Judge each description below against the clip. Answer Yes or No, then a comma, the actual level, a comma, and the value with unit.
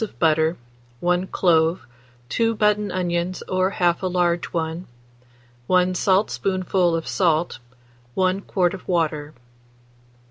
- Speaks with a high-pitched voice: No, medium, 180 Hz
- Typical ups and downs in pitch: No, narrow, 1.9 semitones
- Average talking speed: No, slow, 115 wpm